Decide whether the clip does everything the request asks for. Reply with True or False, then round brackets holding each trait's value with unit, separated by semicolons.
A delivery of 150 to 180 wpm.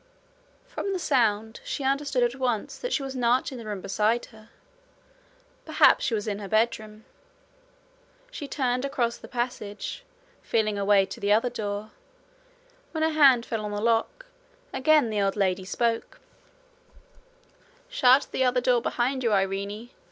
True (160 wpm)